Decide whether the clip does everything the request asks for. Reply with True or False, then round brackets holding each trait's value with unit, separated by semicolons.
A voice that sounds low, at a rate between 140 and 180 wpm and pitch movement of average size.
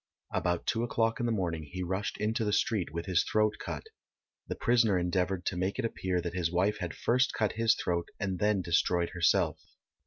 False (95 Hz; 205 wpm; 3.9 semitones)